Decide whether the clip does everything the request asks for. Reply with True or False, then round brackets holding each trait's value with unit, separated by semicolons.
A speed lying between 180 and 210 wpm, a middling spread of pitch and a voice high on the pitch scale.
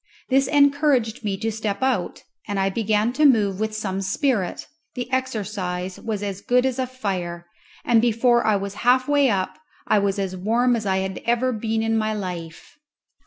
True (185 wpm; 4.2 semitones; 220 Hz)